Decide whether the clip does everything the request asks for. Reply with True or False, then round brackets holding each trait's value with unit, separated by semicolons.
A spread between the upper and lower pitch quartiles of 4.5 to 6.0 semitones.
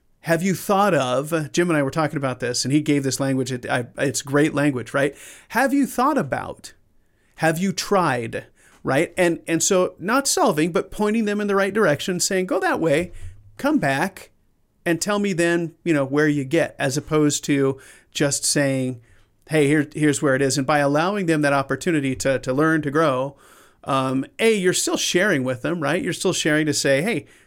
True (4.8 semitones)